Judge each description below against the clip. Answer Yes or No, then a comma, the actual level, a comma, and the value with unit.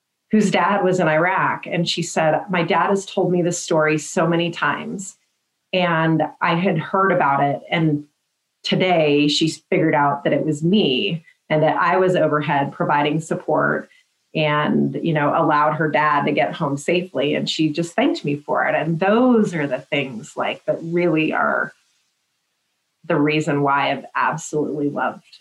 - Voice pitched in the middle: Yes, medium, 160 Hz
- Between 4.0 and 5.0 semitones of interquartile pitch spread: No, average, 3.3 semitones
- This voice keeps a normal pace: Yes, average, 170 wpm